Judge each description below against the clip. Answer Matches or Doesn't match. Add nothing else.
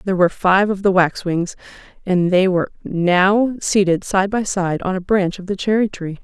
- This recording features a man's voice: Doesn't match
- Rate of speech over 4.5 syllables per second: Matches